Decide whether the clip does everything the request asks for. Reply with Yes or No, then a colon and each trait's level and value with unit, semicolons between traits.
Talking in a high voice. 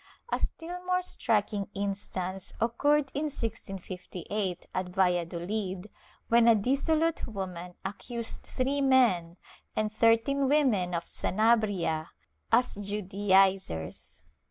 Yes: high, 205 Hz